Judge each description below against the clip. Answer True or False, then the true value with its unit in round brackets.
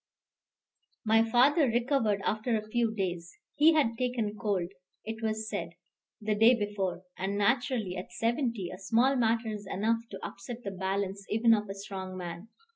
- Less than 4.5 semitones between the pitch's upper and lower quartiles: True (3.1 semitones)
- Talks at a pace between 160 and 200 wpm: True (165 wpm)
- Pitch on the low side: False (215 Hz)